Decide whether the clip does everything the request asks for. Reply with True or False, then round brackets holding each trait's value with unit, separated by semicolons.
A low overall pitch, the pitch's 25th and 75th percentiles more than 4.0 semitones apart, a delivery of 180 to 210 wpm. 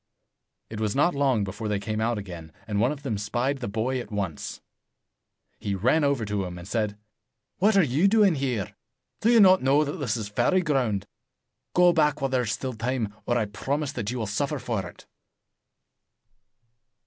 True (120 Hz; 5.5 semitones; 200 wpm)